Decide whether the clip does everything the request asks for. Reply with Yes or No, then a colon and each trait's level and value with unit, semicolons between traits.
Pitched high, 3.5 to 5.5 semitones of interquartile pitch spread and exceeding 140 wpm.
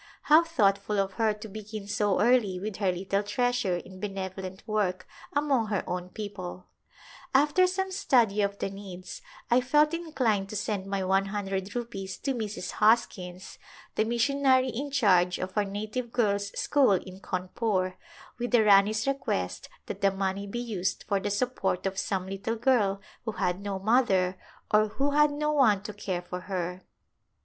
Yes: high, 205 Hz; average, 4.0 semitones; average, 170 wpm